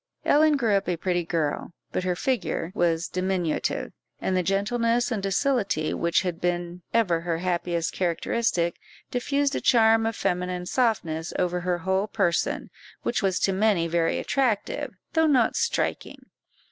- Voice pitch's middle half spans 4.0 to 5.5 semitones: Yes, average, 4.6 semitones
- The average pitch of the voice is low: No, medium, 185 Hz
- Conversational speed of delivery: Yes, average, 150 wpm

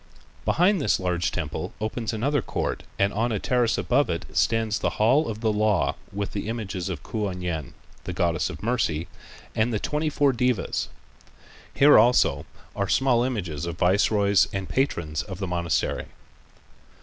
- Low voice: Yes, low, 105 Hz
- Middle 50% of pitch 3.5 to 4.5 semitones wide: No, average, 5.0 semitones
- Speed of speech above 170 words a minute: No, average, 160 wpm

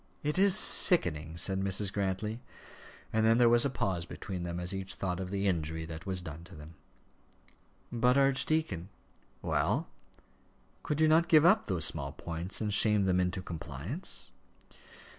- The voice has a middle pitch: No, very low, 95 Hz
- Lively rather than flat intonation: Yes, wide, 6.0 semitones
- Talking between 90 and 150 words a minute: No, average, 165 wpm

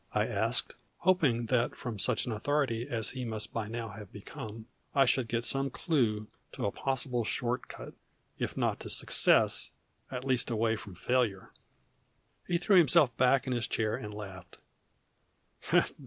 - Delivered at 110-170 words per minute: Yes, average, 160 wpm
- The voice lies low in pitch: Yes, low, 120 Hz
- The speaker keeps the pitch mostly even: No, average, 3.4 semitones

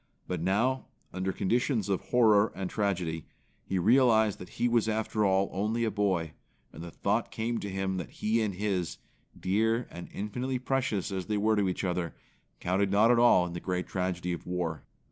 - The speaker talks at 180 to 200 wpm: Yes, average, 190 wpm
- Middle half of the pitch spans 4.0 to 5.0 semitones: No, average, 3.6 semitones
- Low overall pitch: Yes, low, 100 Hz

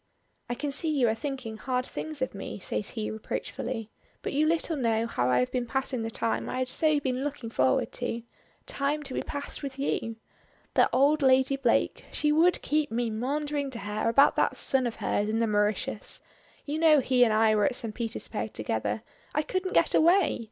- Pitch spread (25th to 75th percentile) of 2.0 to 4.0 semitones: No, average, 4.4 semitones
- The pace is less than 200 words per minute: No, fast, 205 wpm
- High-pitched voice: Yes, very high, 255 Hz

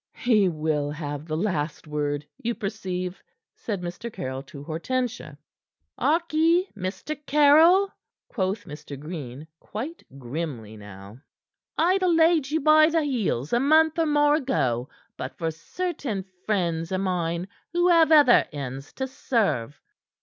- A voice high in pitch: Yes, high, 195 Hz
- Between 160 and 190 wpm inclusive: No, slow, 135 wpm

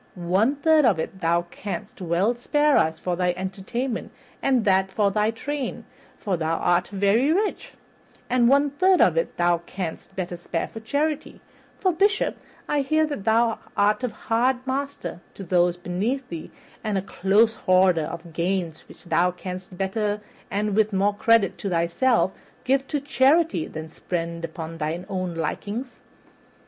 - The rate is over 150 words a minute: Yes, average, 160 wpm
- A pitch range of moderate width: No, wide, 6.5 semitones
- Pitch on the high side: Yes, high, 200 Hz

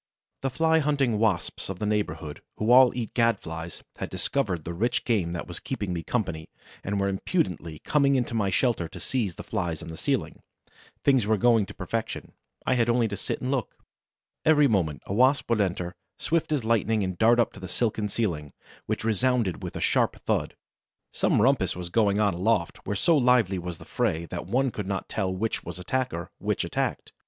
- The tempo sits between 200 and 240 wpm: Yes, fast, 205 wpm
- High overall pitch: No, low, 105 Hz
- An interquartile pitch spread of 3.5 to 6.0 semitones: Yes, wide, 5.5 semitones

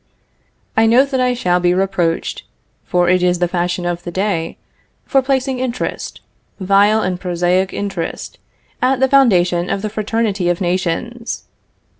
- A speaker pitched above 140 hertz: Yes, high, 190 Hz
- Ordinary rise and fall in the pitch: Yes, average, 4.7 semitones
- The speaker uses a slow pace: No, average, 150 wpm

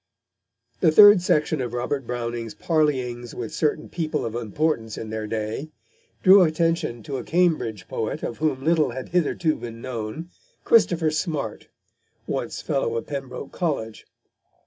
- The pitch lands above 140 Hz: No, low, 135 Hz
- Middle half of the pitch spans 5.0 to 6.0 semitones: Yes, wide, 5.6 semitones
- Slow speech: No, average, 145 wpm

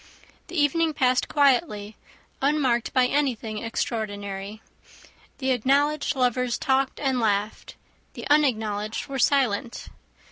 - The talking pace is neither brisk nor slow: No, slow, 105 wpm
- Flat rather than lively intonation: No, average, 4.4 semitones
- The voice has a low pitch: No, very high, 250 Hz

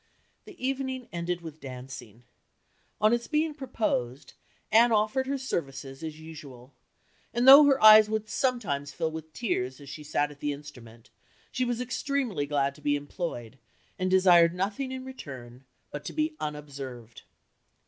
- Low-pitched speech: No, medium, 165 Hz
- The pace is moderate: Yes, average, 155 wpm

